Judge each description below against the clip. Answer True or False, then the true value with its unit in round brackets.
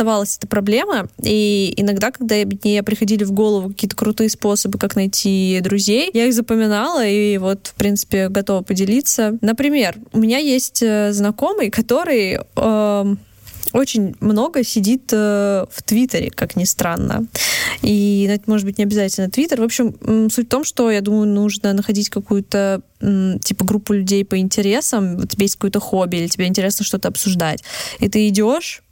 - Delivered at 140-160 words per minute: True (155 wpm)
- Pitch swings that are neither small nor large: False (2.0 semitones)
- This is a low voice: False (210 Hz)